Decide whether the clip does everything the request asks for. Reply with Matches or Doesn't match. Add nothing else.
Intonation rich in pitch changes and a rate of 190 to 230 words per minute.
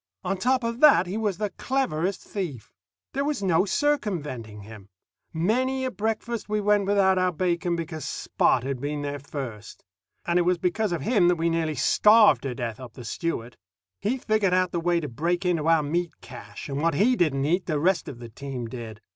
Matches